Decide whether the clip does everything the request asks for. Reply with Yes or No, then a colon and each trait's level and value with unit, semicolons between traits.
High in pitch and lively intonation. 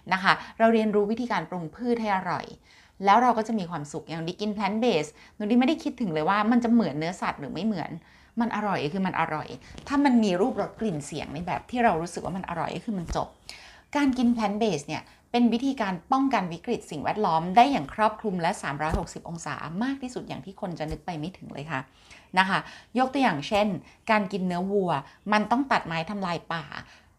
Yes: high, 200 Hz; wide, 5.9 semitones